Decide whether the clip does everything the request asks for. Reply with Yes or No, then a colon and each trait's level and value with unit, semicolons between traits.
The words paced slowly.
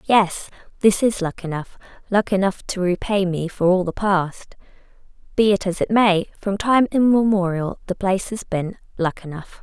No: average, 170 wpm